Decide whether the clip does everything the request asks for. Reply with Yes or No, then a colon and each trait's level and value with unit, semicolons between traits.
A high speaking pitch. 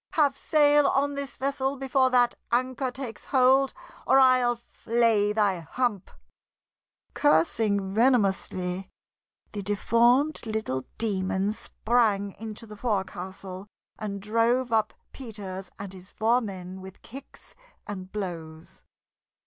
Yes: high, 220 Hz